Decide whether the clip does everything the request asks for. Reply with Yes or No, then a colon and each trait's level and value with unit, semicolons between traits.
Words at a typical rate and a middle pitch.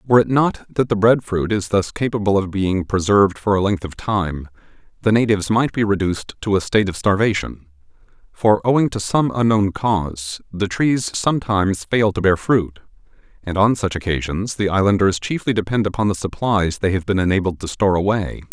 No: average, 190 wpm; low, 100 Hz